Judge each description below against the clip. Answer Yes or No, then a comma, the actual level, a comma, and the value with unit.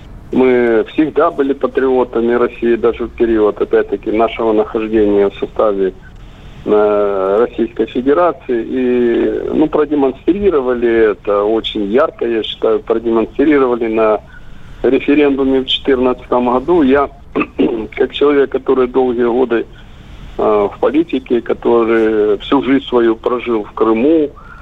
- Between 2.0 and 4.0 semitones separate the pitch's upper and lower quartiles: Yes, average, 3.5 semitones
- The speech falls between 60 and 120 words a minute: Yes, slow, 110 wpm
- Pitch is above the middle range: No, low, 120 Hz